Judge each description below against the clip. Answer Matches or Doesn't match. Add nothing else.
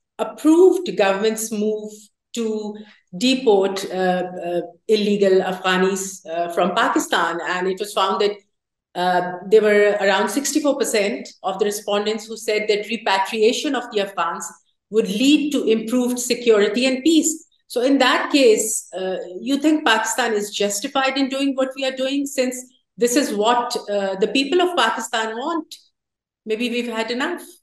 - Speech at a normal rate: Matches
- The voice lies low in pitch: Doesn't match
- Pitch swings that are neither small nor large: Matches